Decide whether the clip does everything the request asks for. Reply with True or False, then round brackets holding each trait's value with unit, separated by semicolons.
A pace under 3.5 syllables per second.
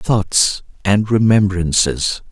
True (3.0 syllables/s)